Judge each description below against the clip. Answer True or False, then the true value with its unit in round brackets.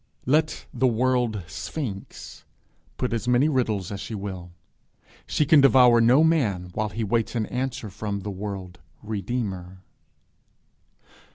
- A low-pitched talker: True (110 Hz)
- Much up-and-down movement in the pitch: False (4.5 semitones)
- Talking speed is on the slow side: True (130 wpm)